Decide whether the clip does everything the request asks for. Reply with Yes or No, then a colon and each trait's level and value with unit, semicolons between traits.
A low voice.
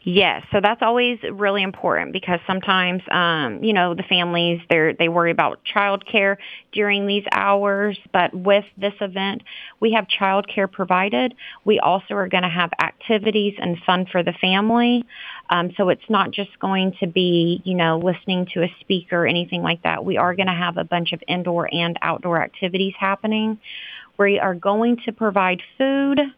No: high, 195 Hz